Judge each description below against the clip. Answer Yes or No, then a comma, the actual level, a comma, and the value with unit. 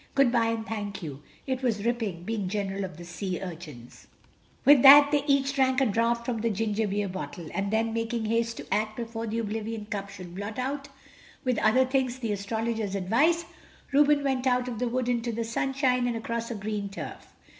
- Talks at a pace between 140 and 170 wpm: No, average, 200 wpm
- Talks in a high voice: Yes, high, 230 Hz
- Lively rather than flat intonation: No, average, 3.6 semitones